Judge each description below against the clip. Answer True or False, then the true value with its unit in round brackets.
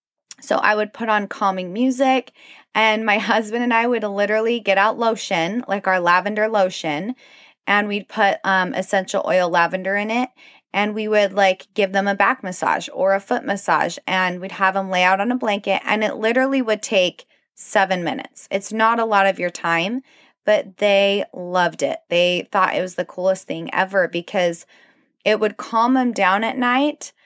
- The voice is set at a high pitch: True (205 Hz)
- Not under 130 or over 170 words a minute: False (190 wpm)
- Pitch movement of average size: True (3.3 semitones)